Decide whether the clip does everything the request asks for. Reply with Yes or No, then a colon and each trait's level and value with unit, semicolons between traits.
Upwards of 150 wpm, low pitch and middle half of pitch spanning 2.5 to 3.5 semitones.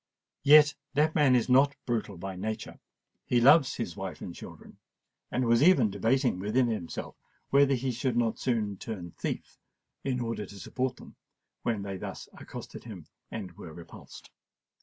No: average, 160 wpm; low, 120 Hz; average, 4.6 semitones